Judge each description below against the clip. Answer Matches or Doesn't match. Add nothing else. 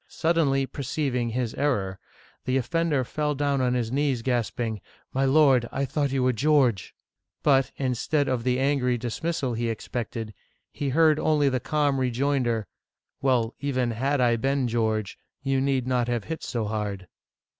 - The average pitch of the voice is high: Doesn't match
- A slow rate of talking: Doesn't match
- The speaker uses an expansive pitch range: Doesn't match